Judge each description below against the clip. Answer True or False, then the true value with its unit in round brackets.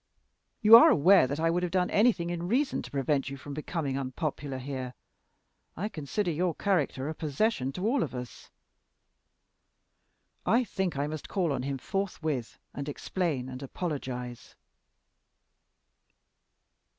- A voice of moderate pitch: True (155 Hz)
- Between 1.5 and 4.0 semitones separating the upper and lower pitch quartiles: False (5.2 semitones)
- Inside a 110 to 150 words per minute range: True (140 wpm)